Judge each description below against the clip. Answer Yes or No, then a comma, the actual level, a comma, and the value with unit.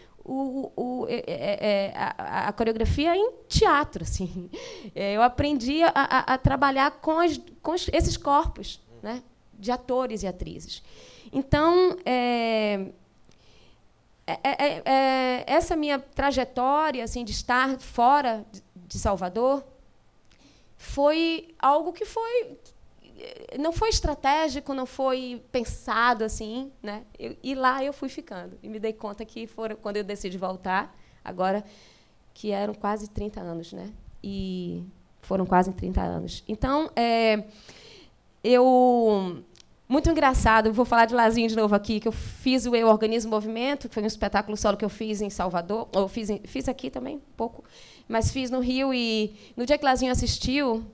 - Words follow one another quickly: No, average, 155 wpm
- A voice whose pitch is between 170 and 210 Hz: No, high, 245 Hz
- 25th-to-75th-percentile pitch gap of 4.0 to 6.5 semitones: Yes, average, 4.6 semitones